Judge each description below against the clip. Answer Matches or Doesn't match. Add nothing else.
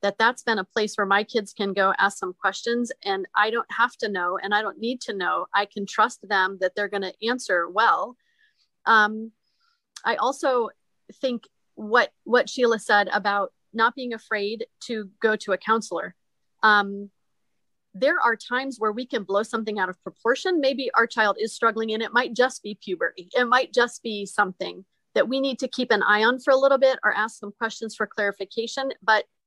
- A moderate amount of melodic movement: Matches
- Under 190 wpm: Doesn't match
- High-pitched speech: Matches